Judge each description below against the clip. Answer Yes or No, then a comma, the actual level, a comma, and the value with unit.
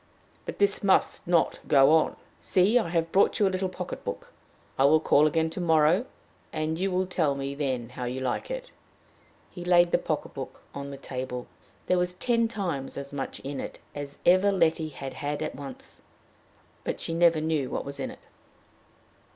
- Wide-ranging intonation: No, average, 4.6 semitones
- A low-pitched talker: No, medium, 160 Hz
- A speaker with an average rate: Yes, average, 190 wpm